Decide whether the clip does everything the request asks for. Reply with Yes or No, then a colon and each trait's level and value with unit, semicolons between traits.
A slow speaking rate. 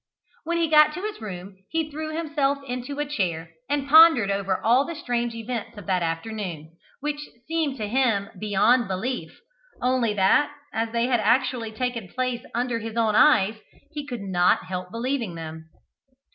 No: average, 170 wpm